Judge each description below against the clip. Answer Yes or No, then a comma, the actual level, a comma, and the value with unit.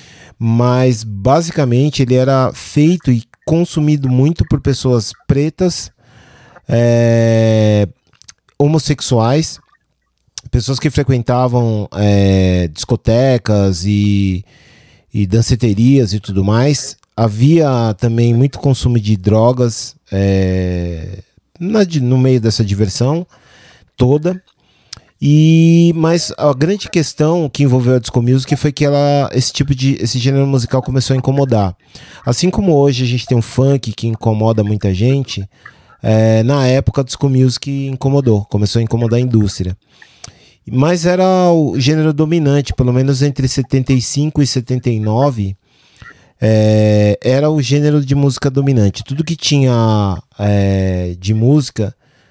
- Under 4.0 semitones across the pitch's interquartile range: No, average, 4.5 semitones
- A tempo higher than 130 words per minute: No, average, 125 wpm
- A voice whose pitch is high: No, low, 125 Hz